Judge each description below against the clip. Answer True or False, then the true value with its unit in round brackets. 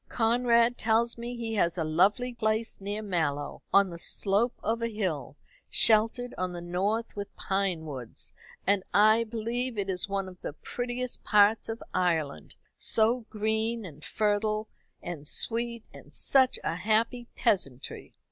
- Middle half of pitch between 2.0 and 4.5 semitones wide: True (4.2 semitones)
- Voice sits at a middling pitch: False (215 Hz)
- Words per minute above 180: False (150 wpm)